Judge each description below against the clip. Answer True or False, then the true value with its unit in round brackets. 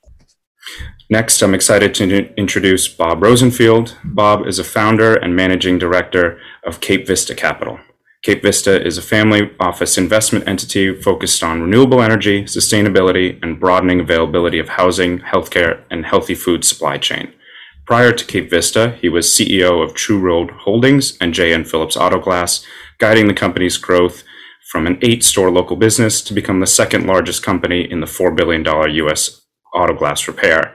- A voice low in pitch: True (95 Hz)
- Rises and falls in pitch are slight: False (3.5 semitones)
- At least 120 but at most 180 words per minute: True (155 wpm)